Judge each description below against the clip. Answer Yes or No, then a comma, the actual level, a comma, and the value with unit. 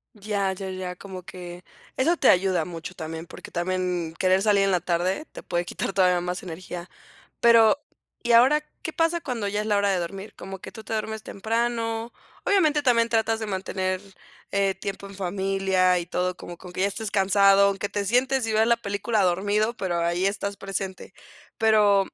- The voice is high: Yes, high, 195 Hz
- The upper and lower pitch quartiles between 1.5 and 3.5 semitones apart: Yes, average, 3.2 semitones